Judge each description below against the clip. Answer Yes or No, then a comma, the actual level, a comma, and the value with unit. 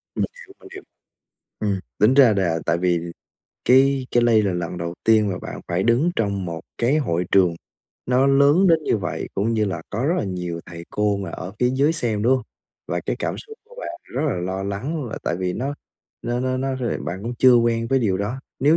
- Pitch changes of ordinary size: No, wide, 5.9 semitones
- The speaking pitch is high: No, low, 115 Hz